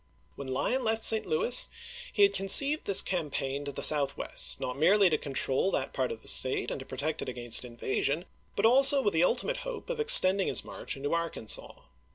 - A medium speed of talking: No, fast, 210 wpm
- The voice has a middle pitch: Yes, medium, 170 Hz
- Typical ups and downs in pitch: No, wide, 8.8 semitones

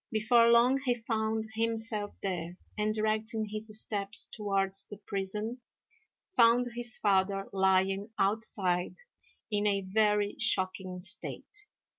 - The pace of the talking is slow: Yes, slow, 115 wpm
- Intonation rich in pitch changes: No, narrow, 2.4 semitones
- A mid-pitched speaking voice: No, high, 210 Hz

